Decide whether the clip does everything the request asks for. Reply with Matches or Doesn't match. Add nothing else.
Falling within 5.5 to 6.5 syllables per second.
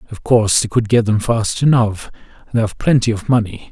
Matches